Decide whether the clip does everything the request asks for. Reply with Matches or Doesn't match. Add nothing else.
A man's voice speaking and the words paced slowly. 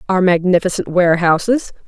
Doesn't match